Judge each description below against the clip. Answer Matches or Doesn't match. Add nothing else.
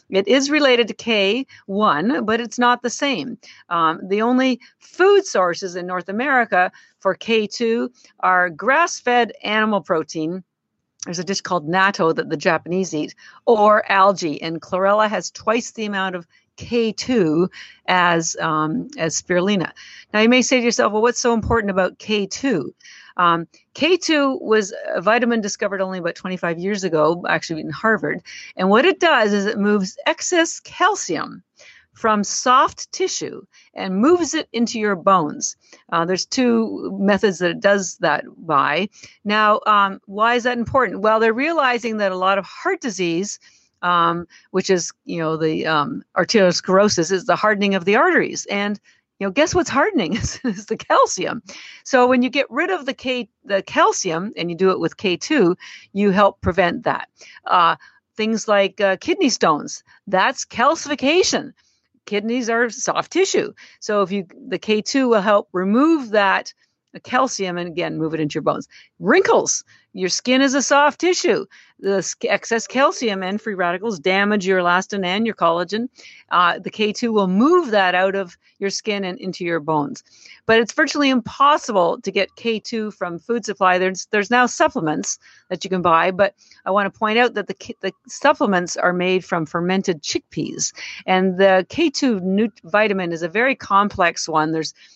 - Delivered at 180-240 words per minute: Doesn't match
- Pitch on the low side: Doesn't match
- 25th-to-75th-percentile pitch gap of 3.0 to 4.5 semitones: Doesn't match